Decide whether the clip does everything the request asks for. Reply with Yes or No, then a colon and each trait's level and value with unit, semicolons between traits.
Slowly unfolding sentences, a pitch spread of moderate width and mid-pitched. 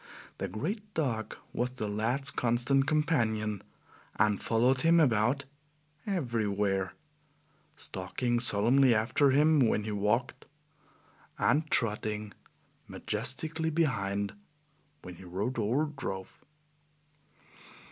No: slow, 95 wpm; average, 5.0 semitones; low, 120 Hz